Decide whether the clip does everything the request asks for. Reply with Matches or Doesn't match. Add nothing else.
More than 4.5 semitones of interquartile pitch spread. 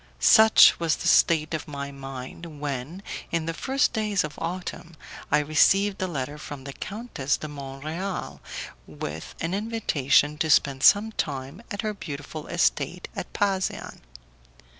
Matches